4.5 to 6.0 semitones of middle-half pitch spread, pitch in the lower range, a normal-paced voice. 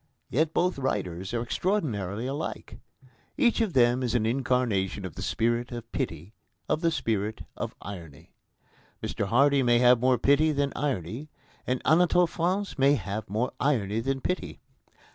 Yes: average, 5.1 semitones; low, 125 Hz; average, 155 wpm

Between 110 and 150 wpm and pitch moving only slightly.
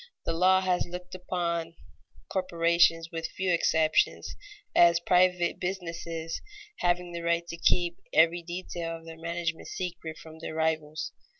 Yes: average, 140 wpm; narrow, 1.3 semitones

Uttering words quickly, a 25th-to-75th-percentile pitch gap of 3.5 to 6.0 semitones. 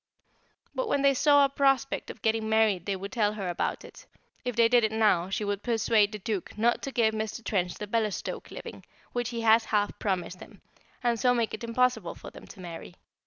No: fast, 215 wpm; average, 2.8 semitones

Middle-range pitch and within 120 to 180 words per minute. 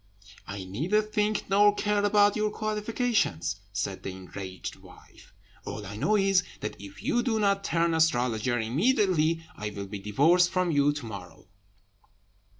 Yes: medium, 165 Hz; average, 150 wpm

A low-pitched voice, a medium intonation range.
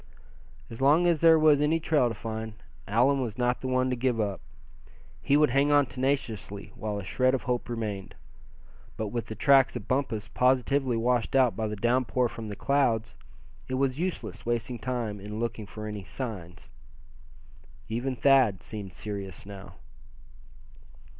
Yes: low, 120 Hz; average, 3.8 semitones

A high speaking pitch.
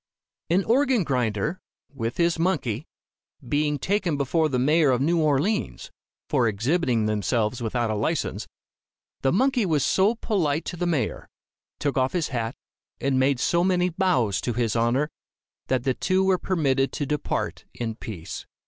No: medium, 145 Hz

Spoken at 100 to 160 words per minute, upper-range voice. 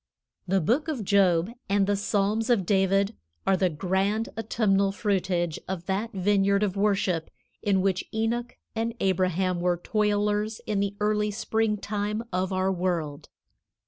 Yes: average, 145 wpm; high, 200 Hz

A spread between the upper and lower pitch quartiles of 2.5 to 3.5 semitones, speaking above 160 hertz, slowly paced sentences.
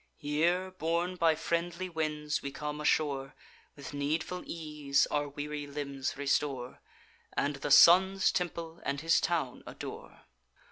No: average, 2.9 semitones; medium, 150 Hz; slow, 130 wpm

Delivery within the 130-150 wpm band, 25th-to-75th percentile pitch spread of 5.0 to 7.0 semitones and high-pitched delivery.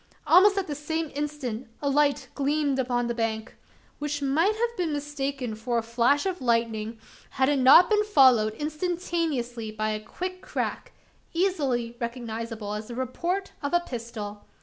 No: average, 160 wpm; wide, 5.4 semitones; very high, 270 Hz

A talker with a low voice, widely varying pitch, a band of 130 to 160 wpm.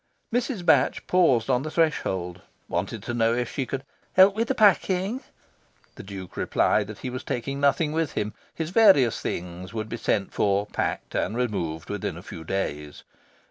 No: low, 125 Hz; wide, 8.6 semitones; average, 180 wpm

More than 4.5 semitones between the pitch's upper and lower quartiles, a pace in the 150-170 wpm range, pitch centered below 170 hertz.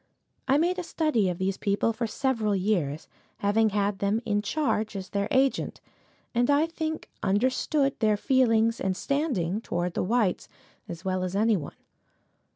No: average, 5.2 semitones; average, 160 wpm; high, 215 Hz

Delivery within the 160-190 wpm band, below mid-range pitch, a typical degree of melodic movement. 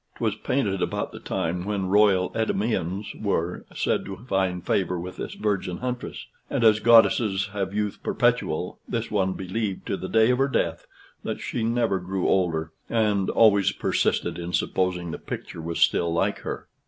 Yes: average, 170 wpm; very low, 95 Hz; average, 3.3 semitones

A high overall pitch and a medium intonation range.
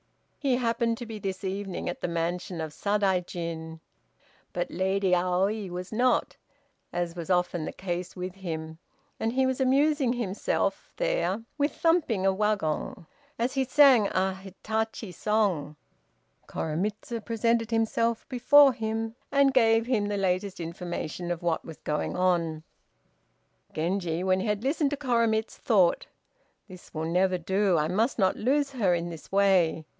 Yes: high, 195 Hz; average, 4.6 semitones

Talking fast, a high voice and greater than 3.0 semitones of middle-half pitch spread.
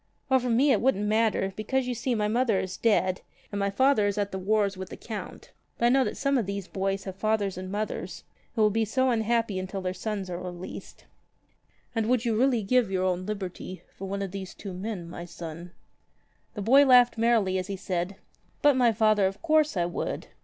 Yes: fast, 220 wpm; high, 210 Hz; average, 3.8 semitones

